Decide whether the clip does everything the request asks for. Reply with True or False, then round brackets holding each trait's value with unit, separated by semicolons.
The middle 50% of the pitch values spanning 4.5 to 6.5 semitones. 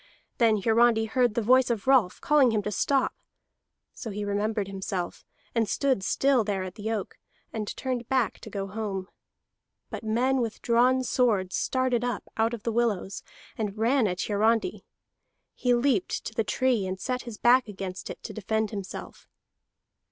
False (3.3 semitones)